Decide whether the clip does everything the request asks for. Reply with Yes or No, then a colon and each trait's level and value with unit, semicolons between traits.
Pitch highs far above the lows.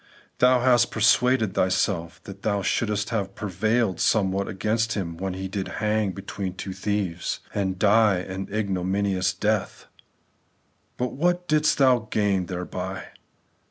No: average, 2.7 semitones